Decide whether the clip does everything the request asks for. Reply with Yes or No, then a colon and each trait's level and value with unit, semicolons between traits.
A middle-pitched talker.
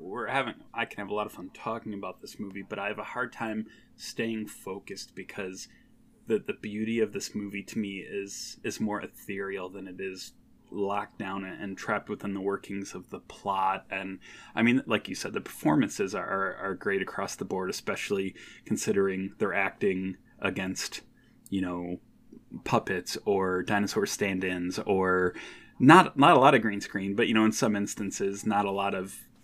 No: low, 100 Hz